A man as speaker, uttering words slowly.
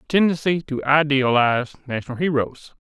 Yes: male; slow, 125 wpm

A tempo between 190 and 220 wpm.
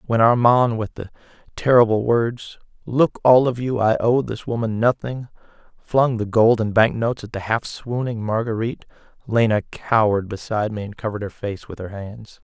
No: average, 180 wpm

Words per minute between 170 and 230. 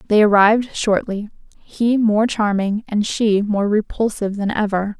No: average, 145 wpm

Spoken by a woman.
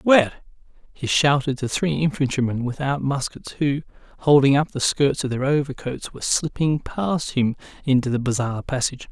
No: male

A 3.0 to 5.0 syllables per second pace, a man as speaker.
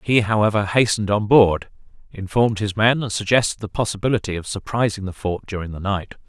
No: 6.0 syllables/s; male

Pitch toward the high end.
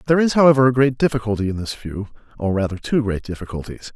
No: low, 115 Hz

